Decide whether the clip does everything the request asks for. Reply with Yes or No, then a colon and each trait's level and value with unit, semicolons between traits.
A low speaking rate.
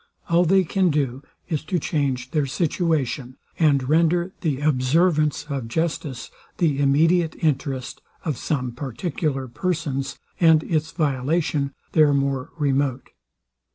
Yes: slow, 120 wpm